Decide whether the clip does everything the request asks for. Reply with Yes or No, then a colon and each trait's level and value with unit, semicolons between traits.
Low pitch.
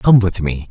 Yes: very low, 95 Hz